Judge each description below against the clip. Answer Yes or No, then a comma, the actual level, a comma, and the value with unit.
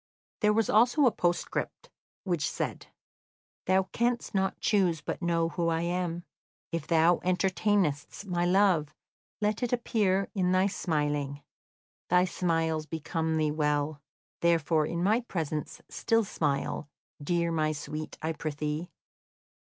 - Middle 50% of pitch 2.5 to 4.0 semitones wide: Yes, average, 3.7 semitones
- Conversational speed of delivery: No, slow, 130 wpm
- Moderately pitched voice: Yes, medium, 170 Hz